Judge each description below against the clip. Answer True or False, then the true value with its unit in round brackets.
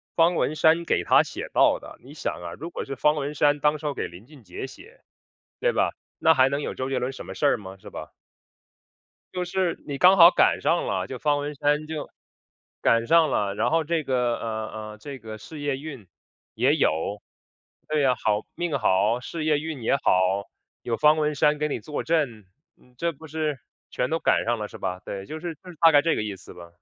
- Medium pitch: True (145 Hz)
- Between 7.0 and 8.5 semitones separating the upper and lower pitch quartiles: False (5.7 semitones)